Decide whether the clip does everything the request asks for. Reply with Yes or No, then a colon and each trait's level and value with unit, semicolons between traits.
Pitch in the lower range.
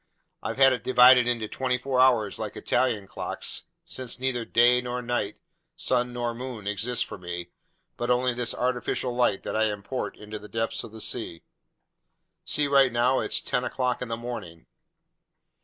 Yes: low, 120 Hz